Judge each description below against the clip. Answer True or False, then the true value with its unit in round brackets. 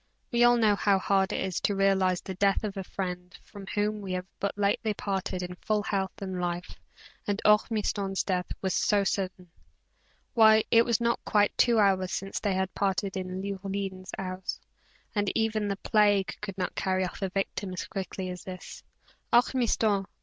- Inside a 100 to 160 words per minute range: False (180 wpm)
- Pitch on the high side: True (195 Hz)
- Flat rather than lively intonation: True (1.8 semitones)